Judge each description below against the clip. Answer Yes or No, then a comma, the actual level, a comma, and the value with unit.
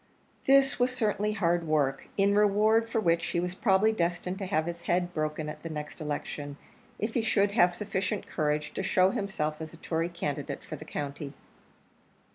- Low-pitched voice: No, medium, 175 Hz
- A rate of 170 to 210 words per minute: Yes, average, 185 wpm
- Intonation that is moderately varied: Yes, average, 5.0 semitones